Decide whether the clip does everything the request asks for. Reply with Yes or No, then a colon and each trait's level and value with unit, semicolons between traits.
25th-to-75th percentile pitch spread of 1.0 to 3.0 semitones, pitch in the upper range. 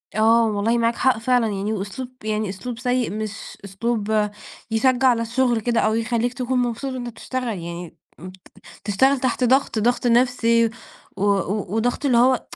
Yes: average, 2.7 semitones; high, 230 Hz